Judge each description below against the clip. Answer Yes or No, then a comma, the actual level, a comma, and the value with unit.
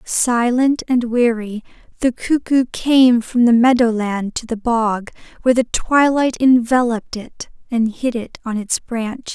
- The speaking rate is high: No, average, 155 wpm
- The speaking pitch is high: Yes, high, 240 Hz